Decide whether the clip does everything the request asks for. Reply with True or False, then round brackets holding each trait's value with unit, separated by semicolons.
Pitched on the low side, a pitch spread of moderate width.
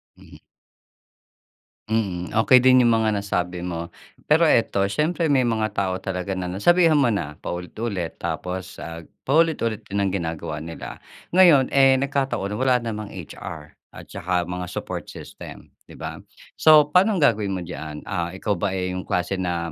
False (100 Hz; 6.5 semitones)